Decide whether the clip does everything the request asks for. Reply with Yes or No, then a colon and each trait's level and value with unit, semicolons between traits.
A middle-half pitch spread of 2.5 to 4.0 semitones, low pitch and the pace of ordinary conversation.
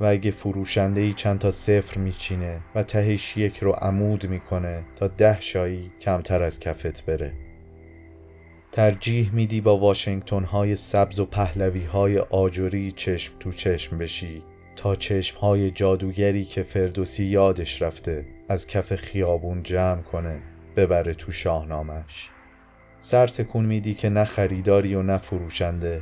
Yes: average, 2.9 semitones; very low, 95 Hz; average, 135 wpm